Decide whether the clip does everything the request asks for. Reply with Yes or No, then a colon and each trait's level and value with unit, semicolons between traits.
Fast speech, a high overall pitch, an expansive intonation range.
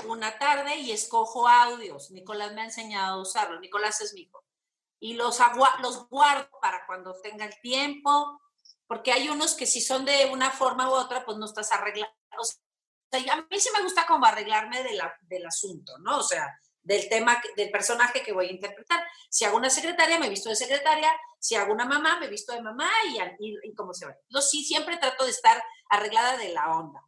Yes: fast, 215 wpm; very high, 250 Hz; wide, 5.8 semitones